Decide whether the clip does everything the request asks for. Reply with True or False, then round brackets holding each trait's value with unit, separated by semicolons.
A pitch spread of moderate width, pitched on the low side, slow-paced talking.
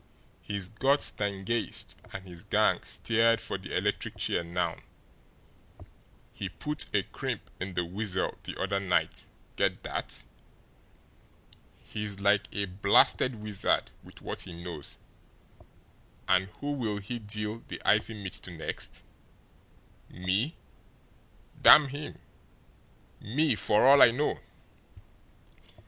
True (3.6 semitones; 105 Hz; 115 wpm)